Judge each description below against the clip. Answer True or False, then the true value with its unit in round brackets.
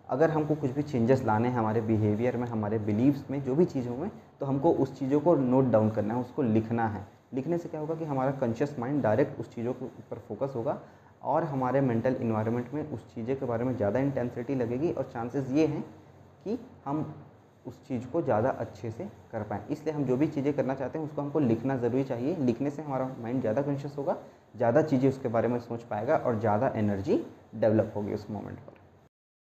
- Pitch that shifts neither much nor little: True (3.5 semitones)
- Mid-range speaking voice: False (125 Hz)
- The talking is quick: True (215 wpm)